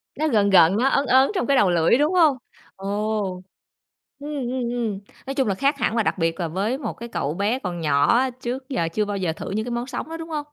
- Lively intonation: Yes, wide, 5.7 semitones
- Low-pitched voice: No, high, 235 Hz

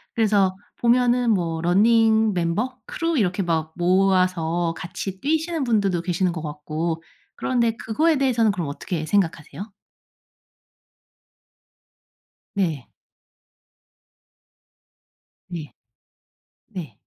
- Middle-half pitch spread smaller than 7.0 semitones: Yes, average, 5.2 semitones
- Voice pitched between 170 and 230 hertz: Yes, high, 190 Hz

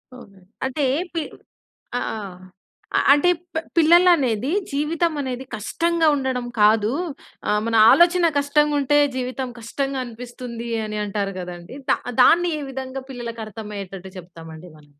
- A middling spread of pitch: No, wide, 5.8 semitones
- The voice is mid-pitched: No, very high, 250 Hz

